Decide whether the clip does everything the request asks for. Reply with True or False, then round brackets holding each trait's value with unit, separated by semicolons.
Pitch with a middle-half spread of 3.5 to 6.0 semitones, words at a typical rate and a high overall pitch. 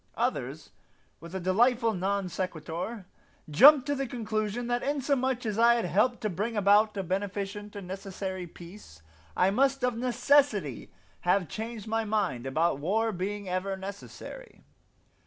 True (4.2 semitones; 145 wpm; 205 Hz)